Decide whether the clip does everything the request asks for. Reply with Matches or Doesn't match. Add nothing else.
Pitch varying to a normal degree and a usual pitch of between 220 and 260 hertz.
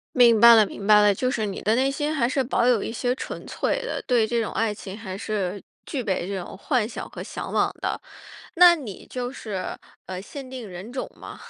Matches